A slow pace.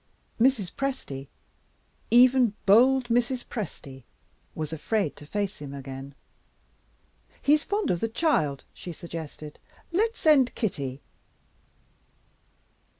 Yes: slow, 100 wpm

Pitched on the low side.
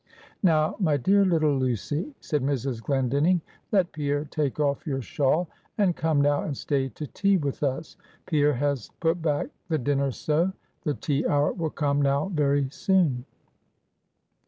No: medium, 145 Hz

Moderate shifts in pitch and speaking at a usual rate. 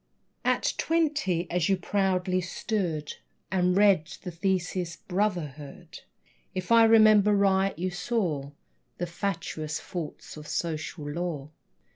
No: average, 3.2 semitones; slow, 115 wpm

